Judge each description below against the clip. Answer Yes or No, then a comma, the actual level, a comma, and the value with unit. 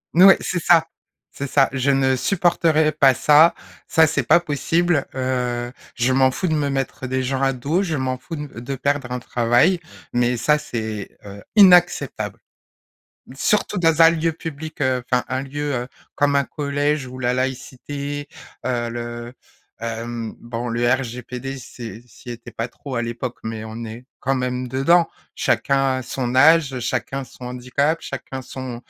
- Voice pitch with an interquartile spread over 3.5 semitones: No, average, 3.2 semitones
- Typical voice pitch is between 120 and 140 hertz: Yes, low, 130 Hz